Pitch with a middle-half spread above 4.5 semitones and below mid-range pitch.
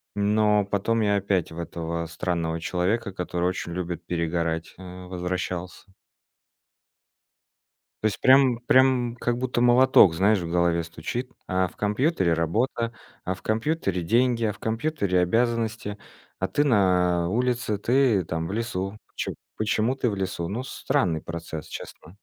Yes: average, 5.1 semitones; low, 100 Hz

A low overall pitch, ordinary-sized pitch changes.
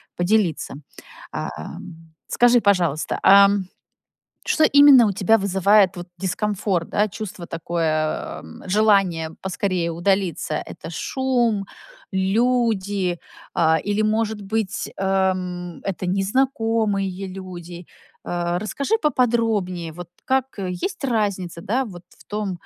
No: high, 195 Hz; average, 3.7 semitones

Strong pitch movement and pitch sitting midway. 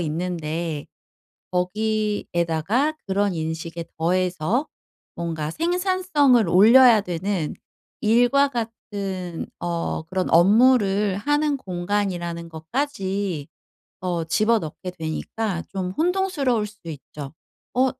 No: wide, 5.7 semitones; high, 195 Hz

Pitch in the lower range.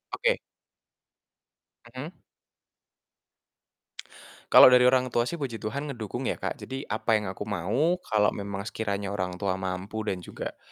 Yes: low, 110 Hz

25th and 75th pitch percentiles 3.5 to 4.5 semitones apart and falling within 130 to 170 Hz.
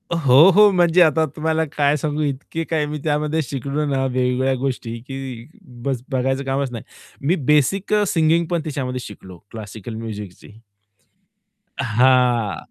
Yes: average, 3.8 semitones; low, 135 Hz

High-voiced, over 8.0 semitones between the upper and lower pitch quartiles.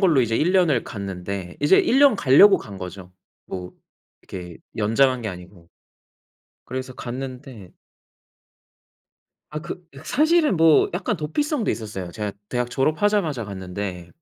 No: low, 125 Hz; wide, 9.0 semitones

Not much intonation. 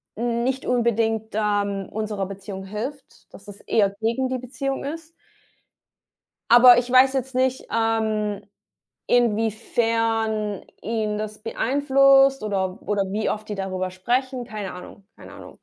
No: average, 3.3 semitones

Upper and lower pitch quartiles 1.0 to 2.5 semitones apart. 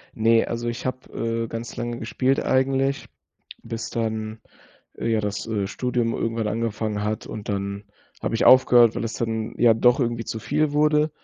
Yes: narrow, 2.2 semitones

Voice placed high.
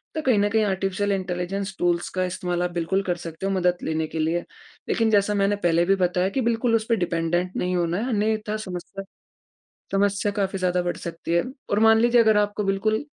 Yes: high, 195 Hz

